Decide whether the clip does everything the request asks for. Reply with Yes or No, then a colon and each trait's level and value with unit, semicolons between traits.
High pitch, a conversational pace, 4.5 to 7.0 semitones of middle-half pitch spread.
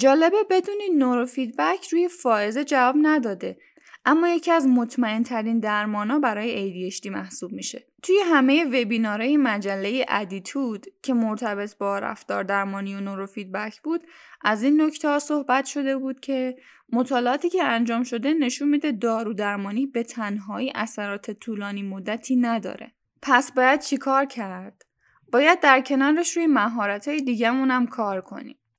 Yes: very high, 250 Hz; average, 140 wpm; wide, 5.4 semitones